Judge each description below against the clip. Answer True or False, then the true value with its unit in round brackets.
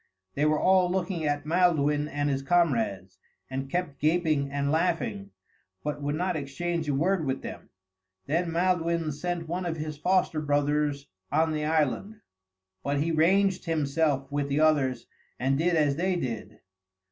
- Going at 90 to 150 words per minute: False (160 wpm)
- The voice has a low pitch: False (155 Hz)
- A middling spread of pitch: True (3.4 semitones)